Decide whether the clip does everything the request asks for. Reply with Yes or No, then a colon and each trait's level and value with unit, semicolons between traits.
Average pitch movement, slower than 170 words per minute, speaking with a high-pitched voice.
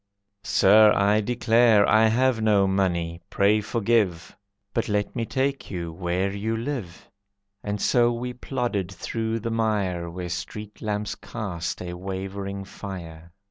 No: average, 3.3 semitones; average, 140 wpm; low, 105 Hz